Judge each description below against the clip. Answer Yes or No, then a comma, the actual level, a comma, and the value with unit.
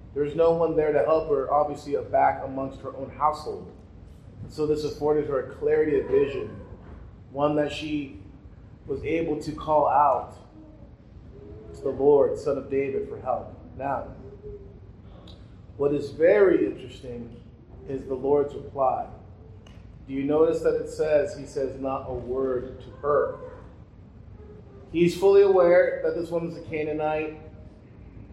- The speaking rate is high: No, average, 145 wpm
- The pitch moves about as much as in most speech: No, wide, 7.6 semitones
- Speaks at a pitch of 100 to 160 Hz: Yes, medium, 140 Hz